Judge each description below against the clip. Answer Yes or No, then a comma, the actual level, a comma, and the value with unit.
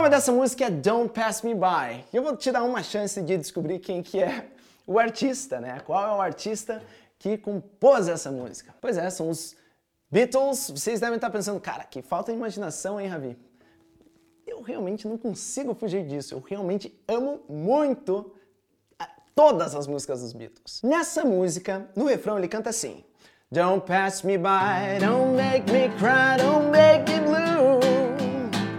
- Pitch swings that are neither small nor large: No, wide, 5.8 semitones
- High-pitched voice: Yes, high, 215 Hz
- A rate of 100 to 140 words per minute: No, average, 170 wpm